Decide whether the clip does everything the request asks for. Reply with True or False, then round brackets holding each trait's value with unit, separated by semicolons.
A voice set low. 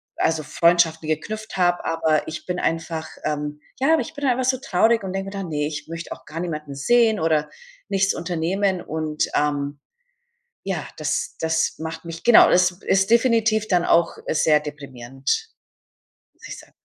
False (165 Hz)